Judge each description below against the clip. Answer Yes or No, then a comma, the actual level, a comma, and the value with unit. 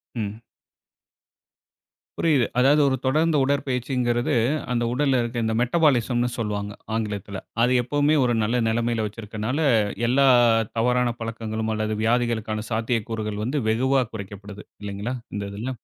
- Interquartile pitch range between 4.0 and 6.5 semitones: No, average, 2.9 semitones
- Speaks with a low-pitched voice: Yes, low, 120 Hz